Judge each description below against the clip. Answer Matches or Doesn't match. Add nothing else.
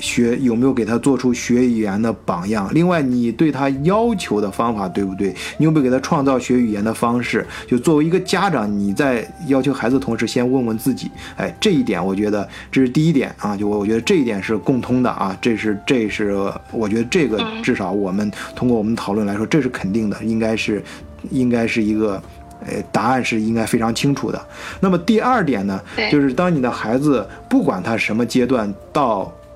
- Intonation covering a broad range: Doesn't match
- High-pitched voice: Doesn't match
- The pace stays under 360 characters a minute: Matches